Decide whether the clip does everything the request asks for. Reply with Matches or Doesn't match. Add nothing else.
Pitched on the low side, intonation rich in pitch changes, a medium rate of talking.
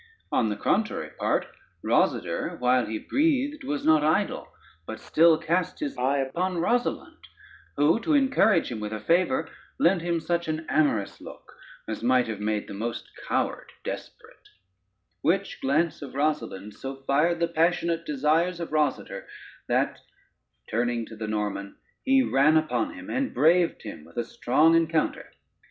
Doesn't match